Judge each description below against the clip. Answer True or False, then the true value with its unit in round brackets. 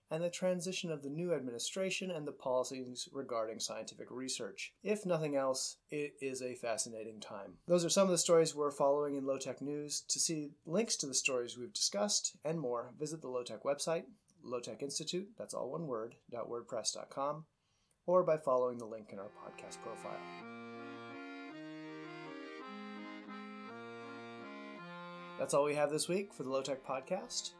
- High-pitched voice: False (140 Hz)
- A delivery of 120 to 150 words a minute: False (165 wpm)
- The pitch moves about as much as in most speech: False (6.3 semitones)